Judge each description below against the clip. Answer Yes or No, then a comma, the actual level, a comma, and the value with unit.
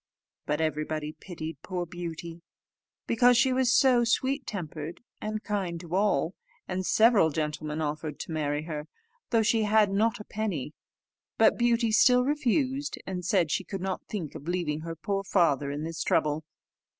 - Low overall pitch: No, medium, 180 Hz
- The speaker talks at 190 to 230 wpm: No, average, 160 wpm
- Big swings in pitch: Yes, wide, 6.0 semitones